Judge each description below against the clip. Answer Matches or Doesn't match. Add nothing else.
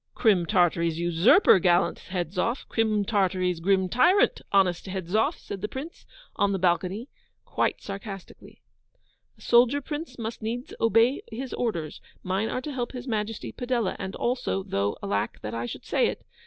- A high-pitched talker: Matches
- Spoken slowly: Doesn't match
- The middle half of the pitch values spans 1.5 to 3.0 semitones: Doesn't match